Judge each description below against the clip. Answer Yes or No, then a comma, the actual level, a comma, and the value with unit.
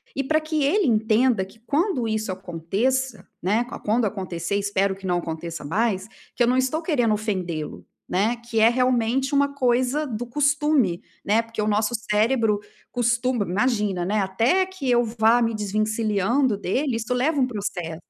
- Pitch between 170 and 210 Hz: No, high, 225 Hz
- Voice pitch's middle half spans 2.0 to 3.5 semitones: No, average, 4.2 semitones